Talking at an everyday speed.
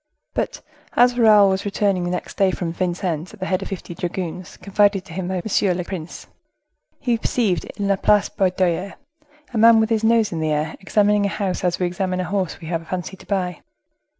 No: fast, 215 wpm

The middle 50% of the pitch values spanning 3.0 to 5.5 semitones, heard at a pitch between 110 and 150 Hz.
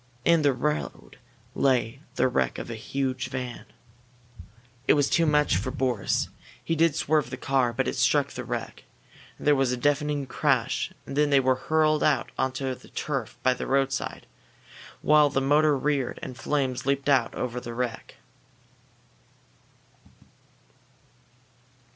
No: narrow, 2.6 semitones; low, 135 Hz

